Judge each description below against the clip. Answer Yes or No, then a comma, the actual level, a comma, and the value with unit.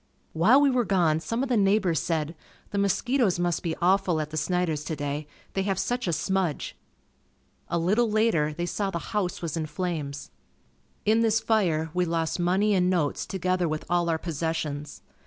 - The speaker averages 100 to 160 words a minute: No, average, 180 wpm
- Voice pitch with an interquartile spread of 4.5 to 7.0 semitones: No, average, 4.0 semitones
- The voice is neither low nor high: Yes, medium, 175 Hz